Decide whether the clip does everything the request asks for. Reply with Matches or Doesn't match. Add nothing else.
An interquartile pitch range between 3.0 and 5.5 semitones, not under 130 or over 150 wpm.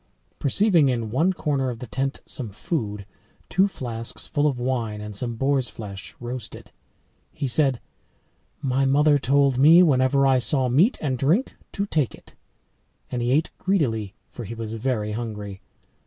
Doesn't match